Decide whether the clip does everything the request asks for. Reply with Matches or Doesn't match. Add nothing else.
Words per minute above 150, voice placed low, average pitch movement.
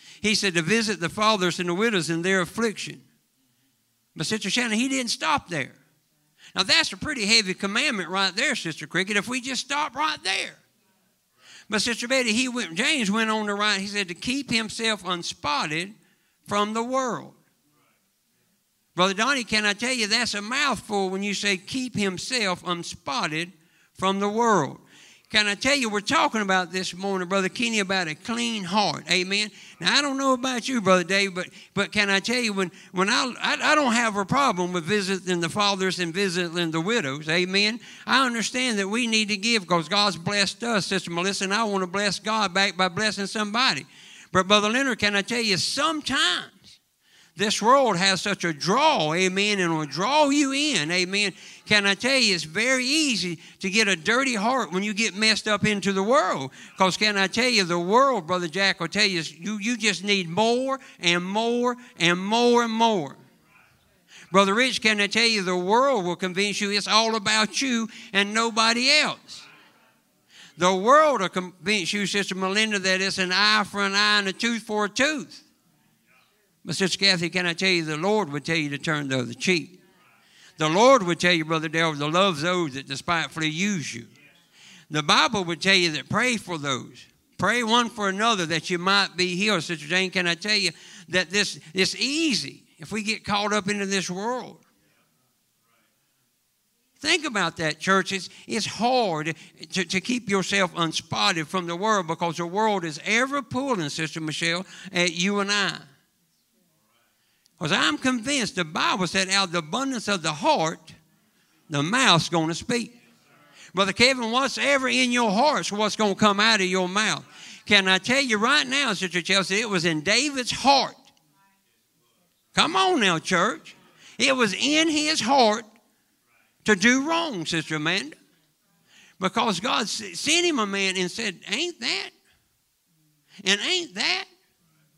Doesn't match